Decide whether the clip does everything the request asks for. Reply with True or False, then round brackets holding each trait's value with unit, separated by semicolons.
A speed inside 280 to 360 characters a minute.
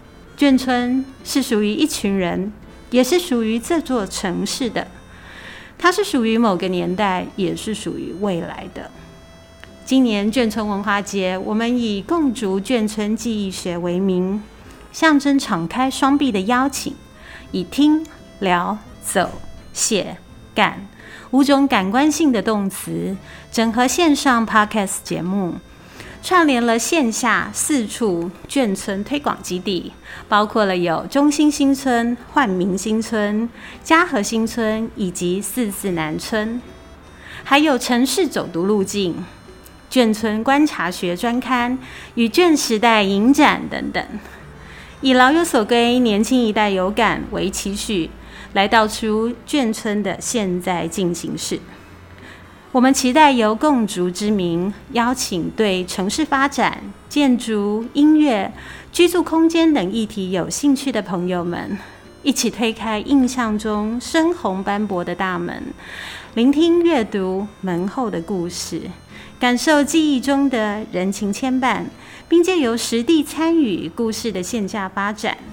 False (200 characters per minute)